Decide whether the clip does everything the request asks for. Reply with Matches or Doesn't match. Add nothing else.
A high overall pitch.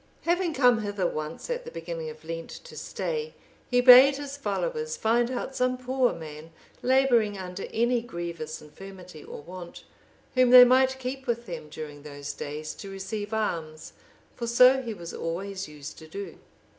Matches